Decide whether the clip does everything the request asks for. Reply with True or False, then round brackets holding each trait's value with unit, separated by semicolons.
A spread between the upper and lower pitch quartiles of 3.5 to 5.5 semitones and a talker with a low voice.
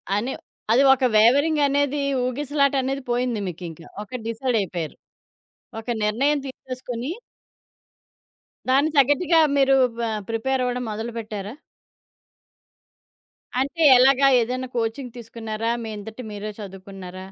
False (4.0 semitones; 245 Hz)